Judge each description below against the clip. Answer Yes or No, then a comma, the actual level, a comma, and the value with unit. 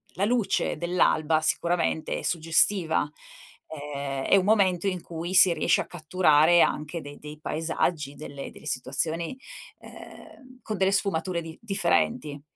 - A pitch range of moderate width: Yes, average, 3.7 semitones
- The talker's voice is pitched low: No, medium, 165 Hz